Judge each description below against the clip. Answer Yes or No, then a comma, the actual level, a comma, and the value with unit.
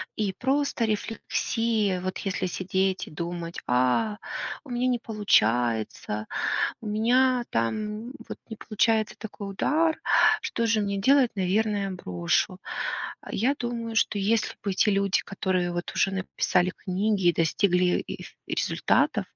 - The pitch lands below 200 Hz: No, high, 205 Hz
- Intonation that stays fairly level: No, average, 3.8 semitones